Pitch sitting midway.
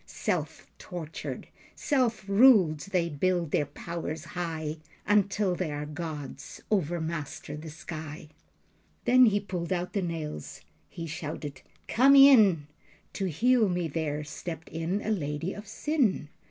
Yes: medium, 170 Hz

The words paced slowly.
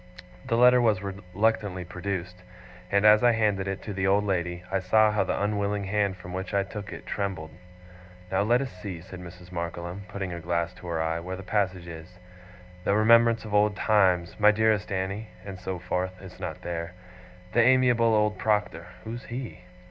No: average, 190 wpm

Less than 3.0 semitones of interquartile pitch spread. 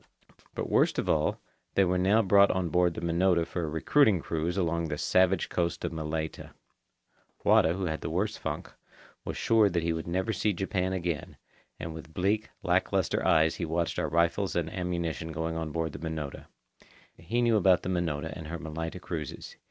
Yes: narrow, 2.5 semitones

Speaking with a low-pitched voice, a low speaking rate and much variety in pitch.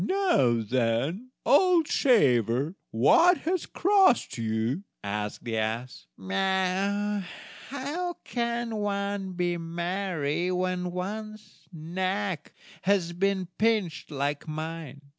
No: medium, 185 Hz; slow, 95 wpm; wide, 6.5 semitones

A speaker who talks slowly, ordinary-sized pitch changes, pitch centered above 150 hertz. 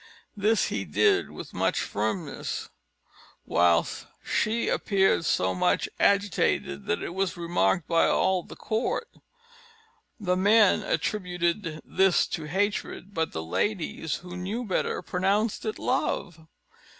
Yes: slow, 125 wpm; average, 3.7 semitones; medium, 185 Hz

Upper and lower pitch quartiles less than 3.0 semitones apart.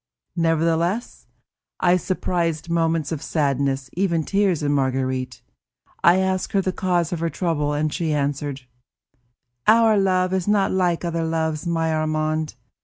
No: average, 3.4 semitones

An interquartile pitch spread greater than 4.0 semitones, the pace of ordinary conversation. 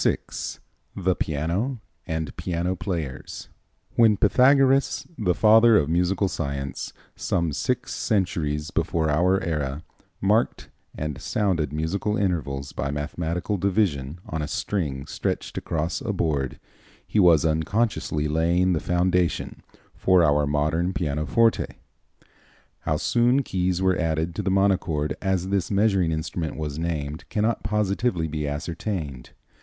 No: average, 4.4 semitones; slow, 125 wpm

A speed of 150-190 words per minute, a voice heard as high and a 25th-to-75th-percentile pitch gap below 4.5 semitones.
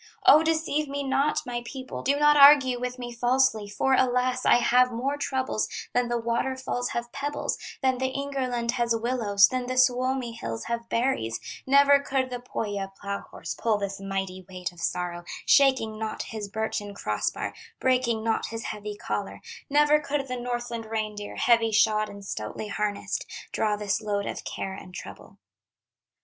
Yes: average, 170 wpm; high, 240 Hz; average, 3.8 semitones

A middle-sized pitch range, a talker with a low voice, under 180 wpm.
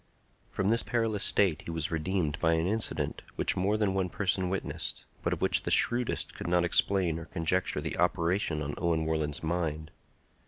No: average, 3.3 semitones; very low, 85 Hz; average, 185 wpm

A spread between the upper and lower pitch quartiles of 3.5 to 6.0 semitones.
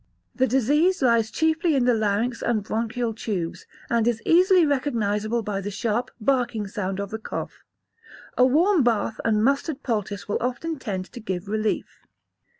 Yes: average, 4.1 semitones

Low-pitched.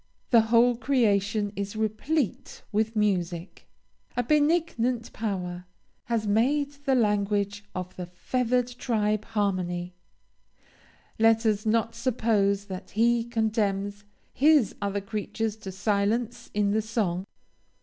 No: high, 215 Hz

